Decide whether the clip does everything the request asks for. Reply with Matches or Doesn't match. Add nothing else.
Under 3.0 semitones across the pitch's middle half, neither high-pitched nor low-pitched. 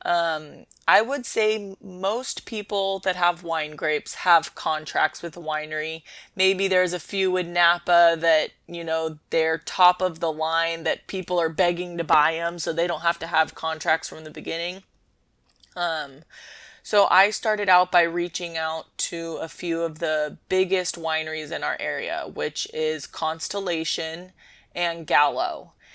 Matches